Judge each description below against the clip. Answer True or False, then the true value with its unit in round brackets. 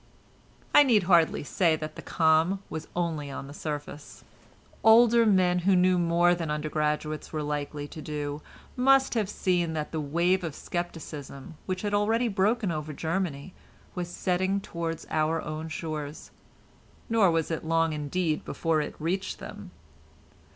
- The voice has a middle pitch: True (165 Hz)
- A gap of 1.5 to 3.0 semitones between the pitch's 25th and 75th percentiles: False (3.6 semitones)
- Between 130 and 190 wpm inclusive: True (150 wpm)